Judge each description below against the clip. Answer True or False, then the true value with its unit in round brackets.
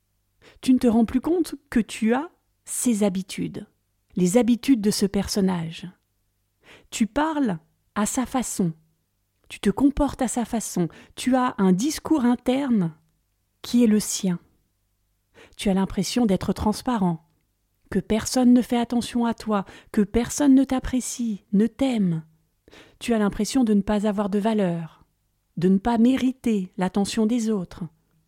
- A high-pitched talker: True (210 Hz)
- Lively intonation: True (6.0 semitones)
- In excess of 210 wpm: False (150 wpm)